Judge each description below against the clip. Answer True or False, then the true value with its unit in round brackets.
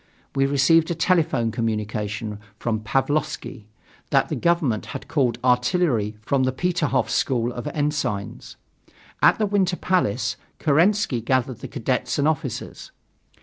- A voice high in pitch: False (135 Hz)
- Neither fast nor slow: False (130 wpm)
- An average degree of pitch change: False (6.1 semitones)